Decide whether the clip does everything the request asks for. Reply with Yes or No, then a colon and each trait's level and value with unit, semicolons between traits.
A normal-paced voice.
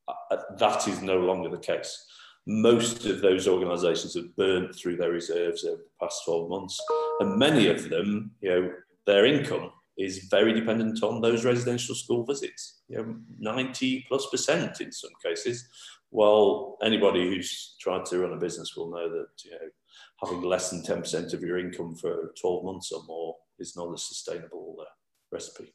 Yes: average, 180 wpm